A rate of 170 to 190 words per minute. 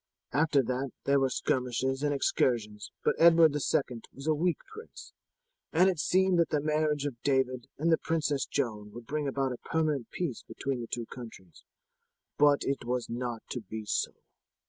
Yes: average, 175 wpm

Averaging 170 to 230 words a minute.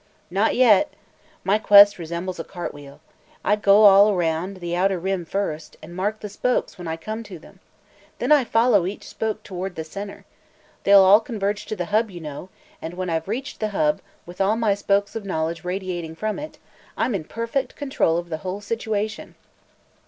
Yes: average, 190 wpm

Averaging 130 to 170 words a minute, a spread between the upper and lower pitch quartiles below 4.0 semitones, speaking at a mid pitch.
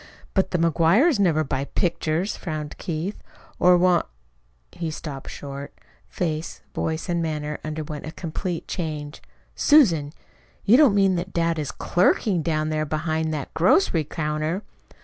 Yes: average, 145 wpm; average, 2.7 semitones; medium, 160 Hz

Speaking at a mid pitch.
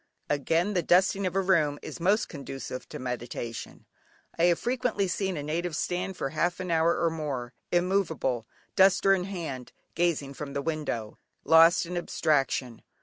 Yes: medium, 165 Hz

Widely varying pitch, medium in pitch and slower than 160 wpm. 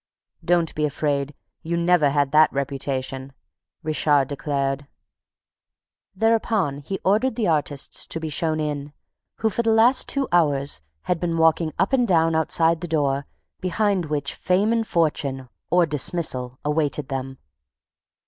No: average, 4.0 semitones; medium, 155 Hz; average, 140 wpm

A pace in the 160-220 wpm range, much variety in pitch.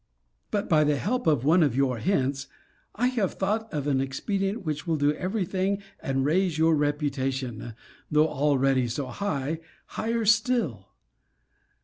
No: average, 150 wpm; wide, 6.3 semitones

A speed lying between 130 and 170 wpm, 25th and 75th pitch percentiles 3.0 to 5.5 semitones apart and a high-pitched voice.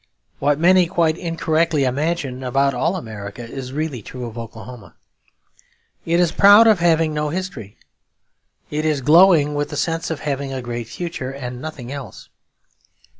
No: average, 155 wpm; average, 4.7 semitones; medium, 145 Hz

